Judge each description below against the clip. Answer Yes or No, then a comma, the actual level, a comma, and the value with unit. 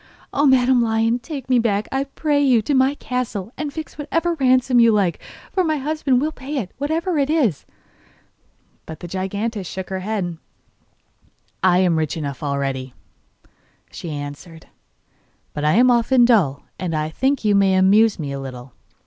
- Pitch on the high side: Yes, high, 220 Hz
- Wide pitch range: Yes, wide, 7.6 semitones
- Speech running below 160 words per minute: No, average, 170 wpm